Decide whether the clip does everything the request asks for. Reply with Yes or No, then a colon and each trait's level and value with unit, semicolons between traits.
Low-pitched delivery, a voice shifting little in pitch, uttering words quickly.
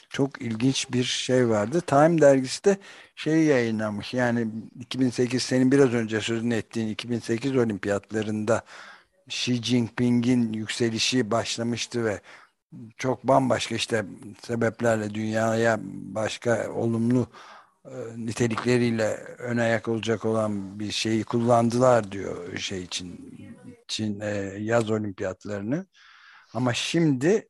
No: low, 115 Hz; narrow, 2.3 semitones; average, 105 wpm